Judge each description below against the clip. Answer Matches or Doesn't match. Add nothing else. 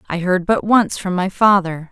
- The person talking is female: Matches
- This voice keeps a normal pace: Doesn't match